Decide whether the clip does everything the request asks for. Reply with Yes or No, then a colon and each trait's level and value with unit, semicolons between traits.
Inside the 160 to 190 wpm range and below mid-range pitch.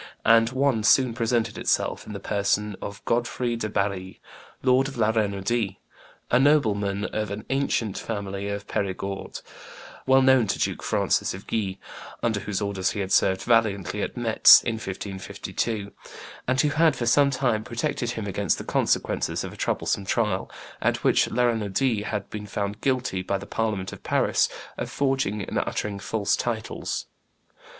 Yes: average, 165 wpm; low, 110 Hz